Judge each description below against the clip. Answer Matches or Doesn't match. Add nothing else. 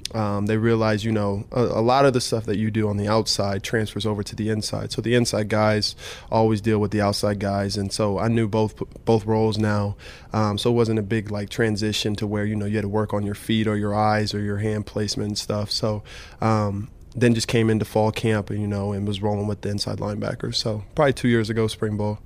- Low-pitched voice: Matches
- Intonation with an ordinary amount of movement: Doesn't match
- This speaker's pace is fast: Matches